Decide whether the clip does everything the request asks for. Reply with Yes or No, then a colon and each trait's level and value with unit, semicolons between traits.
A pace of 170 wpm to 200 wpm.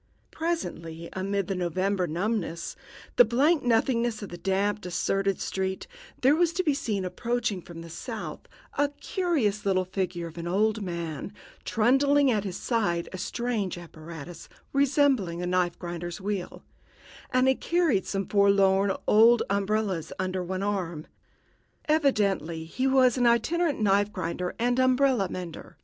No: average, 145 wpm